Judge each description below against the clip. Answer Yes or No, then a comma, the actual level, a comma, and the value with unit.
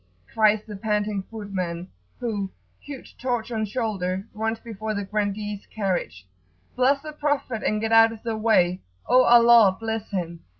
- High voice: Yes, high, 215 Hz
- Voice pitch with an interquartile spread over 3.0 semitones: No, narrow, 2.6 semitones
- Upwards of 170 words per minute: No, average, 155 wpm